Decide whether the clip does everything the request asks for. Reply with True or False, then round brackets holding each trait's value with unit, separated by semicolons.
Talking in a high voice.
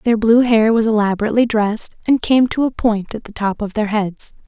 True (220 Hz)